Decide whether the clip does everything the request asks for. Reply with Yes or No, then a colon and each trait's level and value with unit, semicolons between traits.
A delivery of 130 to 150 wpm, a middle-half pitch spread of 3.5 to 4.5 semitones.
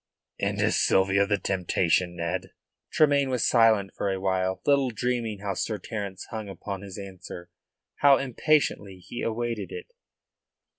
Yes: average, 145 wpm; average, 4.2 semitones